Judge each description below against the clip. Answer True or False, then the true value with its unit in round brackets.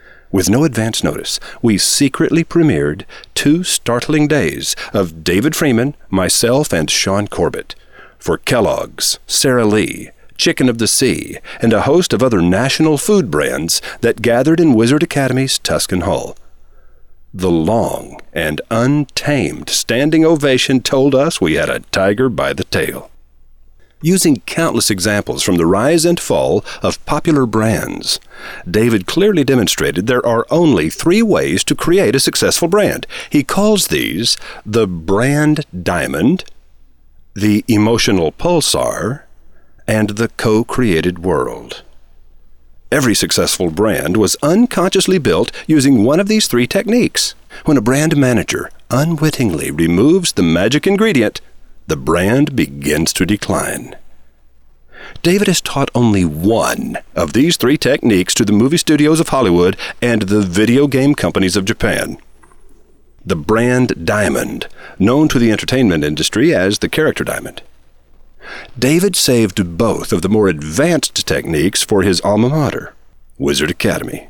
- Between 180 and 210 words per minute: False (135 wpm)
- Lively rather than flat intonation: True (9.0 semitones)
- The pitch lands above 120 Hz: False (115 Hz)